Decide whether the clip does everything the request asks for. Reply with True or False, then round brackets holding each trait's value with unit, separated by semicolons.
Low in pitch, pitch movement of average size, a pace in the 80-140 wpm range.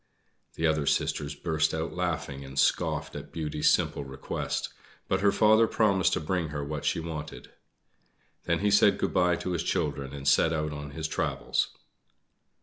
False (80 Hz; 3.5 semitones; 170 wpm)